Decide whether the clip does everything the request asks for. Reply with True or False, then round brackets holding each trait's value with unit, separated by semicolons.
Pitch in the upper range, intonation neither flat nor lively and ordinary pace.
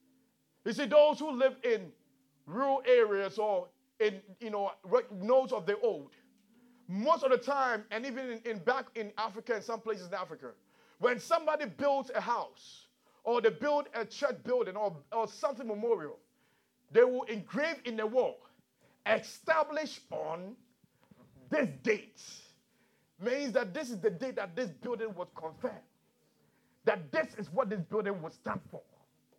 True (240 Hz; 4.2 semitones; 155 wpm)